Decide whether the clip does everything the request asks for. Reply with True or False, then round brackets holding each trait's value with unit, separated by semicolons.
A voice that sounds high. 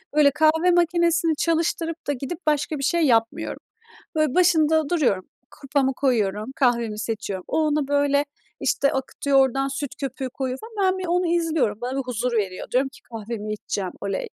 True (275 Hz)